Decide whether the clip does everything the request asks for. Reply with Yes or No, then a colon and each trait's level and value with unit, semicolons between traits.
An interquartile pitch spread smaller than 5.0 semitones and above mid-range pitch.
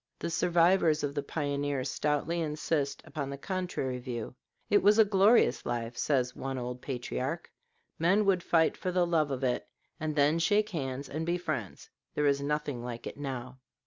No: average, 4.4 semitones; medium, 145 Hz